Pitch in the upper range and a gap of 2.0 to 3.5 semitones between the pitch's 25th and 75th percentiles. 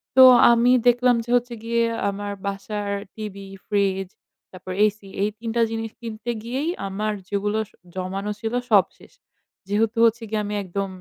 Yes: high, 215 Hz; average, 2.7 semitones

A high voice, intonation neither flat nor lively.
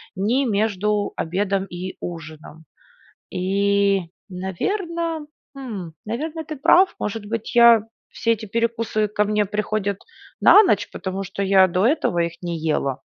Yes: high, 205 Hz; average, 3.7 semitones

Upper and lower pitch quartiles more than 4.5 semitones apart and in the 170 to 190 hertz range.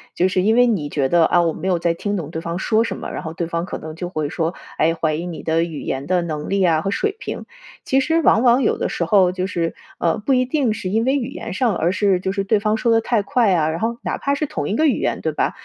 Yes: average, 5.3 semitones; medium, 185 Hz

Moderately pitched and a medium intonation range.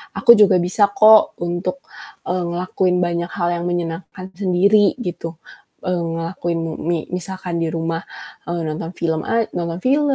No: medium, 175 Hz; narrow, 1.8 semitones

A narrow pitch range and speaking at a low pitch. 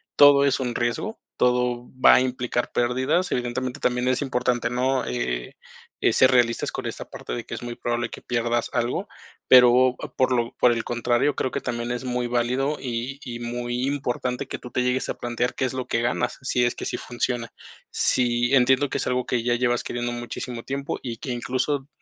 Yes: narrow, 1.2 semitones; low, 125 Hz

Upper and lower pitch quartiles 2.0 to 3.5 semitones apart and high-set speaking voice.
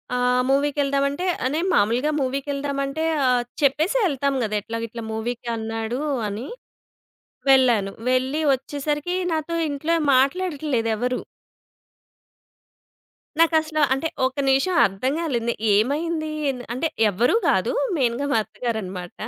No: average, 4.1 semitones; very high, 270 Hz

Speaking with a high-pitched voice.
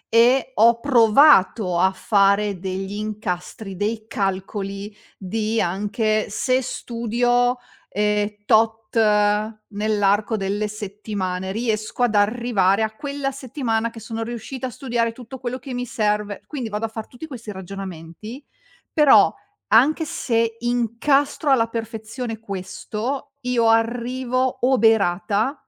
Yes: high, 220 Hz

